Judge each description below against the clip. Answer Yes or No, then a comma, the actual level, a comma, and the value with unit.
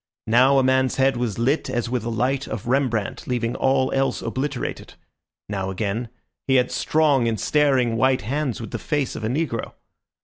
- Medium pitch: No, low, 125 Hz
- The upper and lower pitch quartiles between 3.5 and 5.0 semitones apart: No, average, 2.7 semitones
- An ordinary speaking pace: Yes, average, 180 wpm